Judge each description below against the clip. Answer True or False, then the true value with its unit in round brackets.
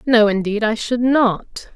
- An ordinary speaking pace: True (170 wpm)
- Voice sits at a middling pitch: False (225 Hz)